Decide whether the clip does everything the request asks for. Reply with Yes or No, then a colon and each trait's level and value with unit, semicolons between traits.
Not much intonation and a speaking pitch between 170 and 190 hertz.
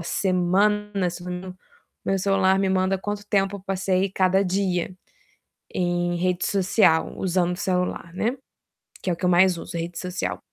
Yes: narrow, 1.6 semitones; medium, 185 Hz